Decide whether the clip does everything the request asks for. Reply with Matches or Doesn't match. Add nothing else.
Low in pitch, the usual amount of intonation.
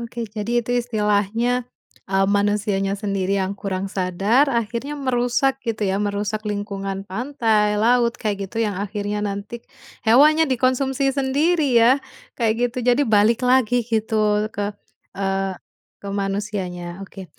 Doesn't match